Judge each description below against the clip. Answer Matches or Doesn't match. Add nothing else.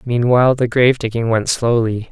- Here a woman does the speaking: Doesn't match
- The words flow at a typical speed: Matches